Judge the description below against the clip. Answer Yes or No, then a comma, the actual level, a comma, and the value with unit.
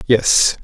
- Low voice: Yes, low, 115 Hz